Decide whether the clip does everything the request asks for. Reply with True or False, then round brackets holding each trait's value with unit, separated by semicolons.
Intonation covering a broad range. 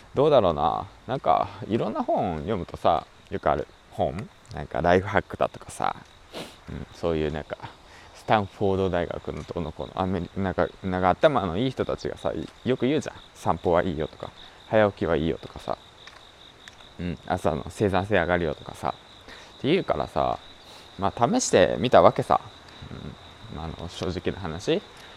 False (2.8 semitones)